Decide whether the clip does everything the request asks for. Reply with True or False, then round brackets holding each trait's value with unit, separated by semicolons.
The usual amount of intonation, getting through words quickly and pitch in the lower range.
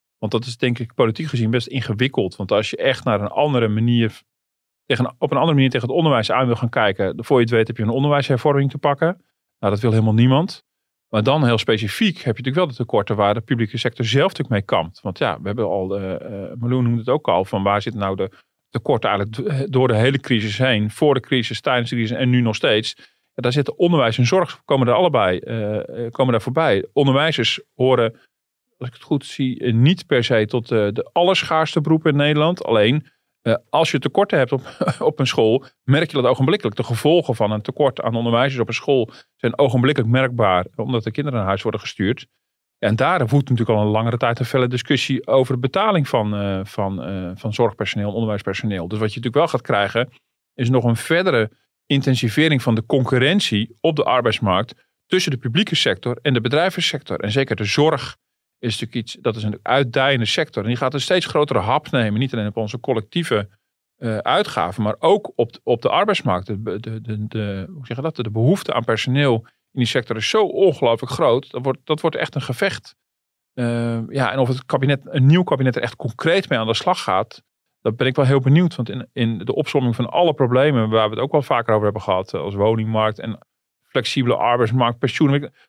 True (3.9 semitones; 210 wpm; 125 Hz)